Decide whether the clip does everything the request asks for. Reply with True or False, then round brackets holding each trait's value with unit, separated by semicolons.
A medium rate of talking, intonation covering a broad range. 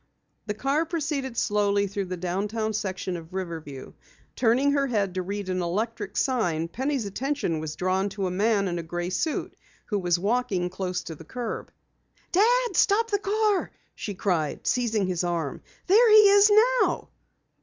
True (165 wpm; 7.1 semitones)